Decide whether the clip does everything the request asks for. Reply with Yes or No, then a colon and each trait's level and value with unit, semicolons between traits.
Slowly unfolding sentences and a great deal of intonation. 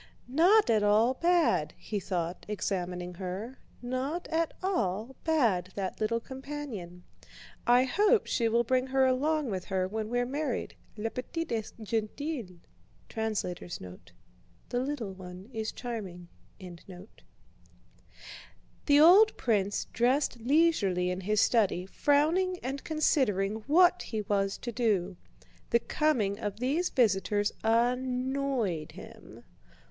Yes: slow, 120 wpm; wide, 6.1 semitones